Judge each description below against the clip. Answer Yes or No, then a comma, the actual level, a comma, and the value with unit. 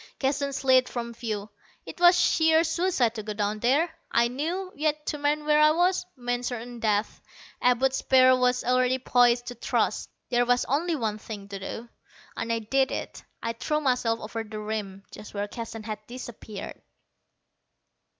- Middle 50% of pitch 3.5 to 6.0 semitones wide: Yes, average, 4.2 semitones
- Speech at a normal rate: Yes, average, 170 wpm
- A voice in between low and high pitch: No, high, 245 Hz